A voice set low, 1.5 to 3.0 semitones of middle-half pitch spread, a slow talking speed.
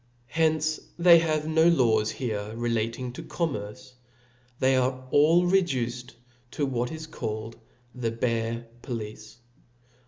No: low, 125 Hz; average, 5.3 semitones; slow, 120 wpm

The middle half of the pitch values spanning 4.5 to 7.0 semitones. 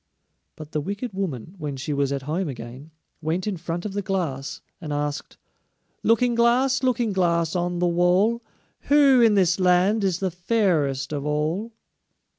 Yes: wide, 5.6 semitones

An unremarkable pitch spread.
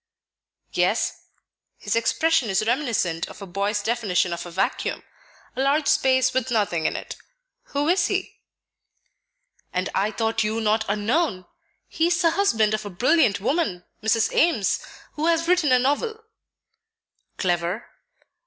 No: wide, 7.3 semitones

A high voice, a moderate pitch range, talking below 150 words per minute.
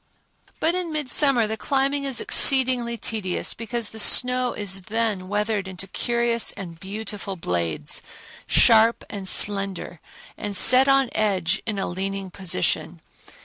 Yes: high, 215 Hz; average, 4.2 semitones; slow, 135 wpm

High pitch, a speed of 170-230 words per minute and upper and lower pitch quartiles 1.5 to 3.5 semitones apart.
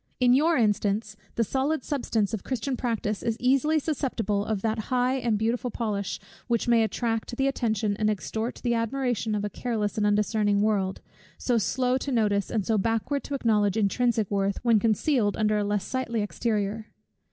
Yes: high, 225 Hz; average, 175 wpm; average, 3.1 semitones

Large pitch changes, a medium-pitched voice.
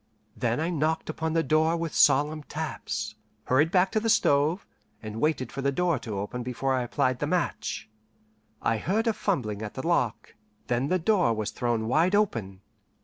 Yes: wide, 5.8 semitones; medium, 145 Hz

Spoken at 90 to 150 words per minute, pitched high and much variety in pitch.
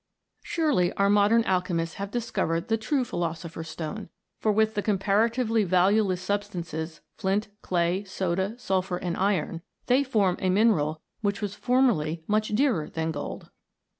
No: average, 145 wpm; high, 195 Hz; average, 4.1 semitones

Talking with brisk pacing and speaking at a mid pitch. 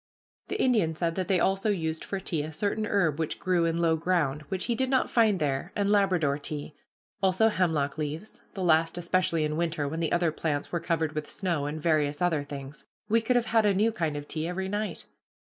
Yes: fast, 220 wpm; medium, 170 Hz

